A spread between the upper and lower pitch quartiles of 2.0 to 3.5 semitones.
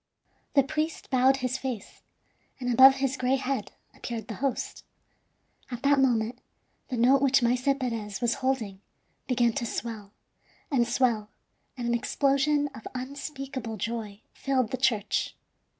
Yes: narrow, 2.6 semitones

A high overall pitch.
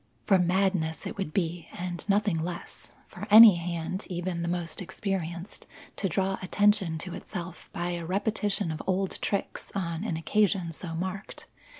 No: medium, 180 Hz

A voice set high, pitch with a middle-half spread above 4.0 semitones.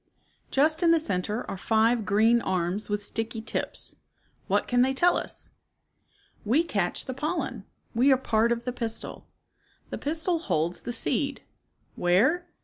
Yes: high, 235 Hz; average, 5.1 semitones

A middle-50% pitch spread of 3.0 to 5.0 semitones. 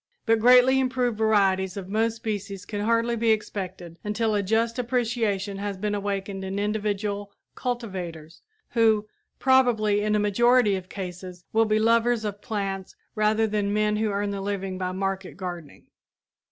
No: narrow, 2.6 semitones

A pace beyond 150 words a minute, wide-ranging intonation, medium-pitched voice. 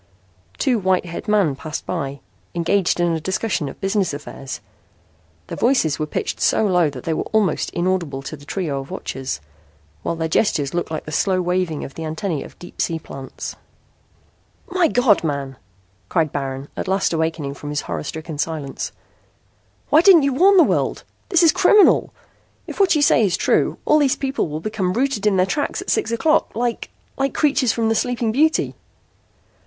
Yes: average, 185 wpm; wide, 7.3 semitones; medium, 180 Hz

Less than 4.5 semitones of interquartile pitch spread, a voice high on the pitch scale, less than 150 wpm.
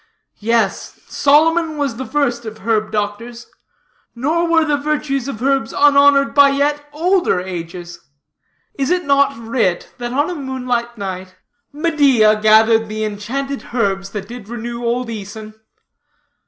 No: average, 4.8 semitones; high, 240 Hz; average, 140 wpm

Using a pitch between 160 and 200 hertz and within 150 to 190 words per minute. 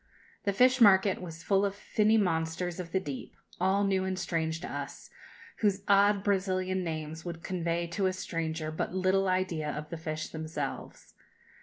Yes: medium, 185 Hz; average, 170 wpm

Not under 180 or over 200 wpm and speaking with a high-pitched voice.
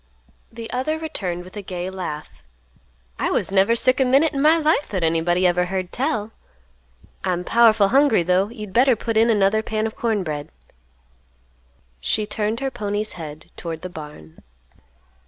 No: average, 165 wpm; high, 210 Hz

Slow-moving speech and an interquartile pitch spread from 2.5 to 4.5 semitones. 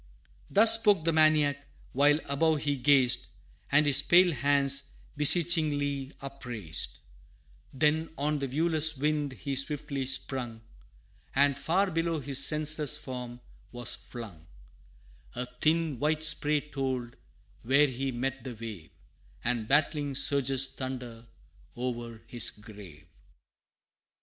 Yes: slow, 115 wpm; average, 3.3 semitones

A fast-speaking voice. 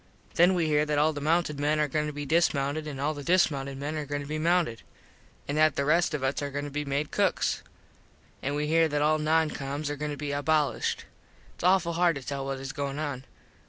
Yes: fast, 245 wpm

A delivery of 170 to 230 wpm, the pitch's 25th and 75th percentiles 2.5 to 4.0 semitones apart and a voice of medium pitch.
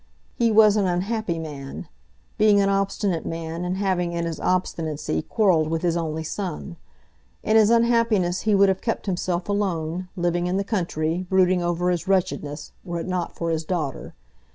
Yes: average, 175 wpm; average, 3.1 semitones; medium, 180 Hz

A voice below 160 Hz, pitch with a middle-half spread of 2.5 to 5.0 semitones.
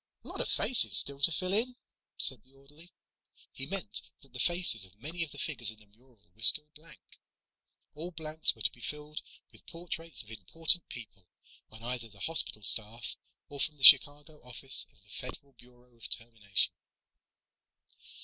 No: low, 135 Hz; wide, 5.6 semitones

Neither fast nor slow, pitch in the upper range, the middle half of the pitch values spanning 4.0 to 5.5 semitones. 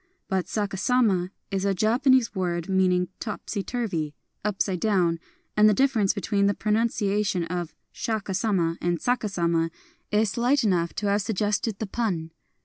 No: average, 170 wpm; high, 200 Hz; average, 3.3 semitones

